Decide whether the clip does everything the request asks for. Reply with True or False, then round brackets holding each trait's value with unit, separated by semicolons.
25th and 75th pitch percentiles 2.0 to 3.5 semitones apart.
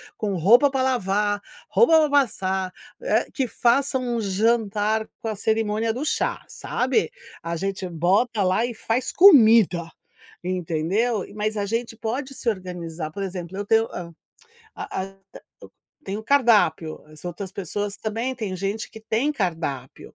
False (4.1 semitones)